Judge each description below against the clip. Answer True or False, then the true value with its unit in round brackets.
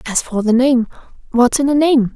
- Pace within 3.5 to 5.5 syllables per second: True (5.1 syllables/s)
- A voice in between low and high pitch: False (250 Hz)